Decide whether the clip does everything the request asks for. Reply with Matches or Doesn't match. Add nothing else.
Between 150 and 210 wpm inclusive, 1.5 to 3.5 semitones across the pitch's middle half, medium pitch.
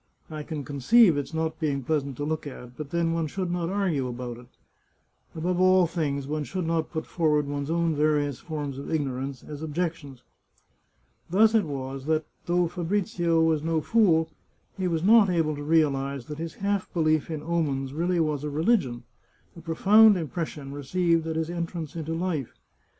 Matches